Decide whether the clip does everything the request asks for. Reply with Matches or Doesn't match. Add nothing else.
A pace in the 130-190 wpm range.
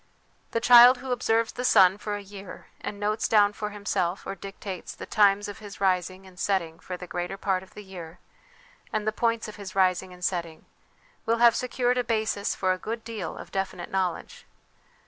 Doesn't match